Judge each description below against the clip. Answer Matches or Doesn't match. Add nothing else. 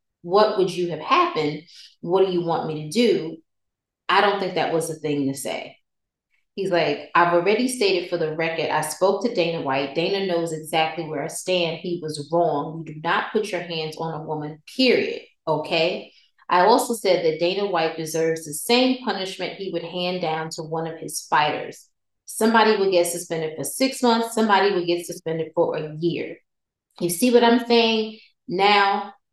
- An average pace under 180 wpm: Doesn't match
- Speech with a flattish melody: Doesn't match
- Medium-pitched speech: Matches